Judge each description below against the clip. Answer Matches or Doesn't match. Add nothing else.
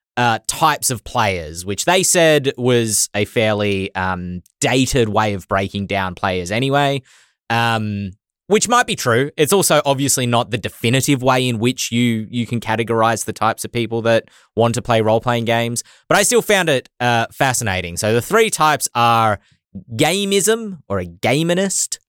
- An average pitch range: Matches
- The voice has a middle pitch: Doesn't match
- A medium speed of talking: Matches